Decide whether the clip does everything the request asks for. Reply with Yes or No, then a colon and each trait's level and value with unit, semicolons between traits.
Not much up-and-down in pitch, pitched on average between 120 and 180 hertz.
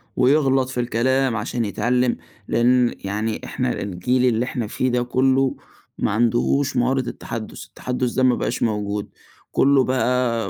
Yes: narrow, 2.2 semitones; low, 125 Hz